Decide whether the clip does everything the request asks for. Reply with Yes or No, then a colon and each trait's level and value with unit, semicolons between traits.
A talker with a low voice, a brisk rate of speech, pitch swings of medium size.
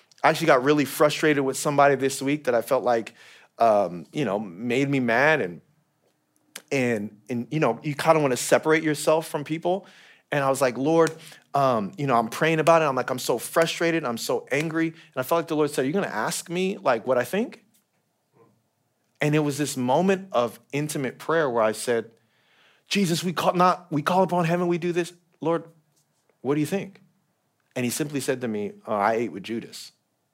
No: medium, 150 Hz; fast, 210 wpm; average, 4.6 semitones